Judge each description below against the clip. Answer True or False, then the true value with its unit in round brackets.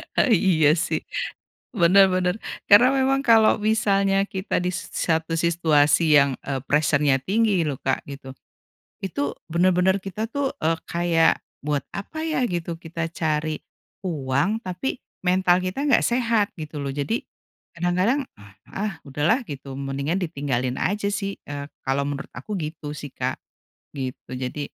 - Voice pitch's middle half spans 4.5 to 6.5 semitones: True (5.5 semitones)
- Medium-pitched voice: True (170 Hz)